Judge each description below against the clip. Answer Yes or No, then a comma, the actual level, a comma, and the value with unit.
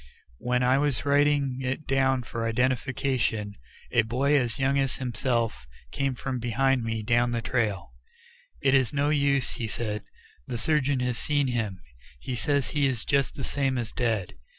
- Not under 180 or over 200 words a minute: No, average, 170 wpm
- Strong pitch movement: No, average, 2.9 semitones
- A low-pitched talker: Yes, low, 125 Hz